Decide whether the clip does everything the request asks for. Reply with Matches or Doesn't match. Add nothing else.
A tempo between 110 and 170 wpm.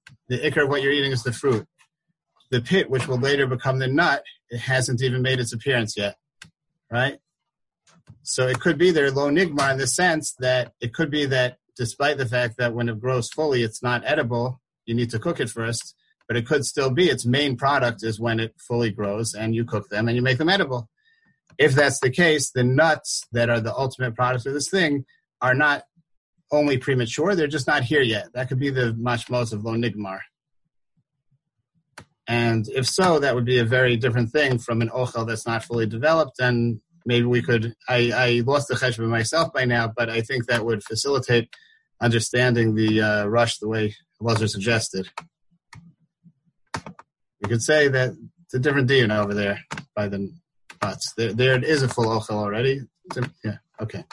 Doesn't match